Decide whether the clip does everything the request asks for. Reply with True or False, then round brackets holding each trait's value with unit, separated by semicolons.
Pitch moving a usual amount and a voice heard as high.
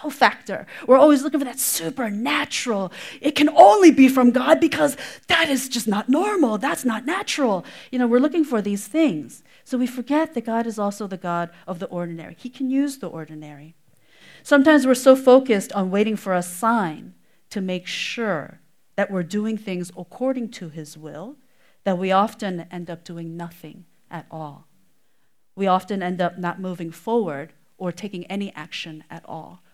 False (6.9 semitones; 205 Hz)